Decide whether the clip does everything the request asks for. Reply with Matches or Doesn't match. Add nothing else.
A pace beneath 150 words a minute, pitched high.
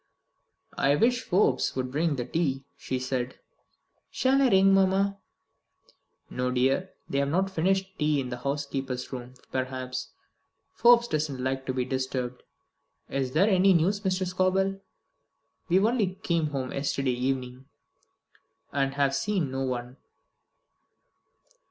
Doesn't match